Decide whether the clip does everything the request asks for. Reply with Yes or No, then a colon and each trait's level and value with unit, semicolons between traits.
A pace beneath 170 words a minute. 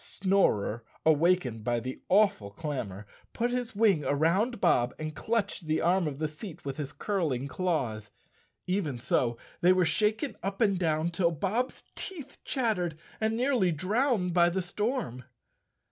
Yes: average, 150 wpm